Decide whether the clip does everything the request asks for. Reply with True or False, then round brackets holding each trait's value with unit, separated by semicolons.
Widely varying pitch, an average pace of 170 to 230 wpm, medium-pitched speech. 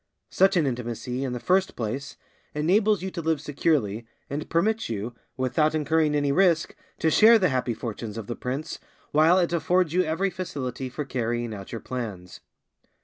True (5.8 semitones; 175 wpm; 145 Hz)